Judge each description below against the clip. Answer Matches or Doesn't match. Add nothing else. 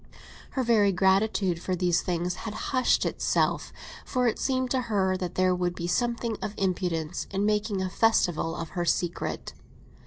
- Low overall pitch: Doesn't match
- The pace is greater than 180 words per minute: Doesn't match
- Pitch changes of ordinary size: Matches